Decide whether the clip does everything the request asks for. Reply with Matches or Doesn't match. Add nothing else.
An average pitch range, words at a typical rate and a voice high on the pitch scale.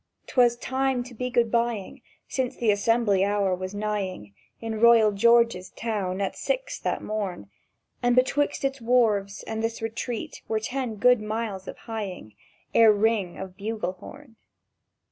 Matches